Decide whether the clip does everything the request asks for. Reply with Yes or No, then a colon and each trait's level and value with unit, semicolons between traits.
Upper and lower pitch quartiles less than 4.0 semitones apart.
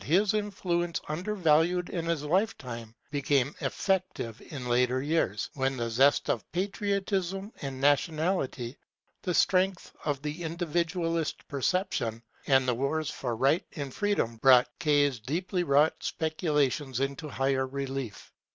No: average, 4.9 semitones